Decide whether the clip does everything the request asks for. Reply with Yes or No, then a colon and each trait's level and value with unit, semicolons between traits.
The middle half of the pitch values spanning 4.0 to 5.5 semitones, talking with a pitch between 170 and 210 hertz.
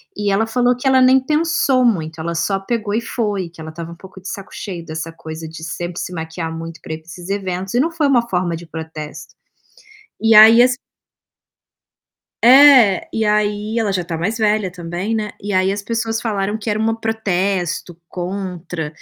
Yes: average, 4.7 semitones; high, 195 Hz